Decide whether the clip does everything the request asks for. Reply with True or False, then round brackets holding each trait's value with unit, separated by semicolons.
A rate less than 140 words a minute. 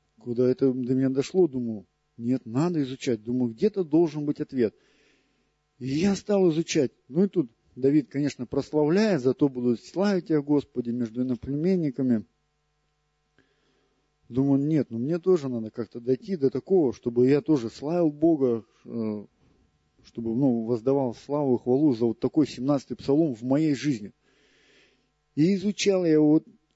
False (145 wpm)